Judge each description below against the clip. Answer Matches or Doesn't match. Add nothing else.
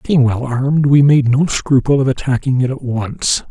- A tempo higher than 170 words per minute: Matches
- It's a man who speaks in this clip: Matches